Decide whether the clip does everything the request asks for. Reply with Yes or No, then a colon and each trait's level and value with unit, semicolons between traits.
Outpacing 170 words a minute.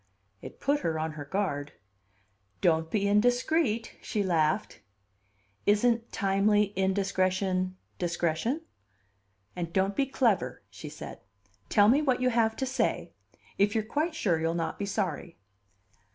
No: slow, 135 wpm